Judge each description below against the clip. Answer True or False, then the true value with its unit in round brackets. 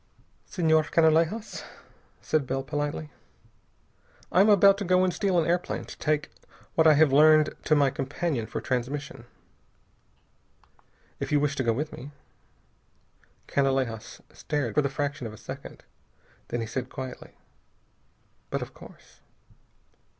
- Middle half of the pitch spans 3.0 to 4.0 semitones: True (3.3 semitones)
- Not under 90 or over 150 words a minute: True (140 wpm)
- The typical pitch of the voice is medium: True (150 Hz)